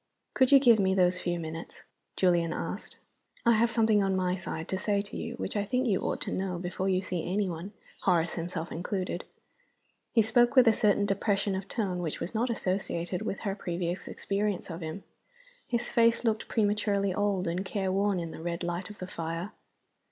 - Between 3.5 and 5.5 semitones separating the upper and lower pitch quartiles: No, average, 3.0 semitones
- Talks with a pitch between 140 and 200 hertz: Yes, high, 190 Hz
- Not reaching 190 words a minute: No, average, 195 wpm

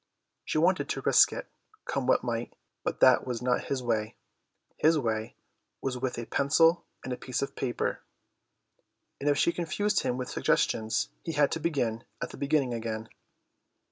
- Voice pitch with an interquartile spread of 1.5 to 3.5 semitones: No, average, 4.2 semitones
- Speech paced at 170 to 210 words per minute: Yes, average, 175 wpm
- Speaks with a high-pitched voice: No, low, 130 Hz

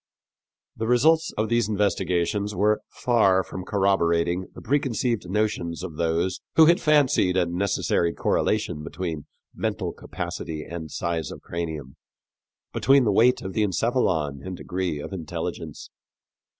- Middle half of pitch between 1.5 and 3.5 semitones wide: No, average, 4.6 semitones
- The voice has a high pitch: No, very low, 95 Hz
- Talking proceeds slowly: Yes, slow, 130 wpm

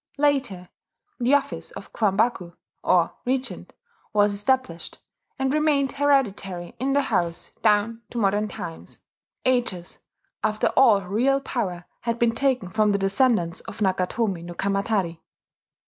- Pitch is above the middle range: Yes, high, 215 Hz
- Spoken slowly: Yes, slow, 130 wpm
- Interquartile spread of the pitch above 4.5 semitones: Yes, wide, 5.5 semitones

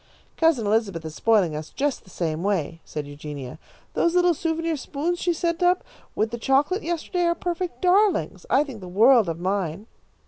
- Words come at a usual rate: Yes, average, 180 wpm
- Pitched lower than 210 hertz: No, high, 240 Hz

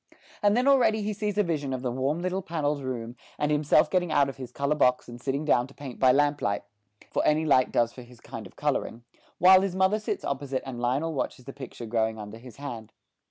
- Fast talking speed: Yes, fast, 230 wpm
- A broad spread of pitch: No, average, 4.9 semitones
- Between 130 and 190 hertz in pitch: Yes, medium, 140 Hz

